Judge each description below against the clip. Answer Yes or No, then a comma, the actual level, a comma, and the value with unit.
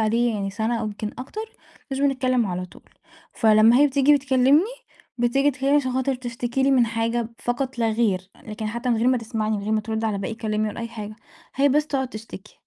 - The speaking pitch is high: Yes, high, 235 Hz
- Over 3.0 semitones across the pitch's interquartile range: Yes, average, 3.4 semitones